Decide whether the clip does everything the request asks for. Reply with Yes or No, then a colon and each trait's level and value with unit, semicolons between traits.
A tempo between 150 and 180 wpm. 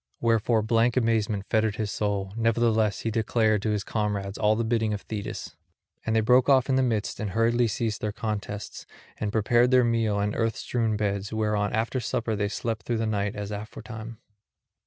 No: average, 190 wpm